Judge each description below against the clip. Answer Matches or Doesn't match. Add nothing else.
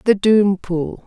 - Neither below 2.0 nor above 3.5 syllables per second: Matches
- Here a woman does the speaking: Matches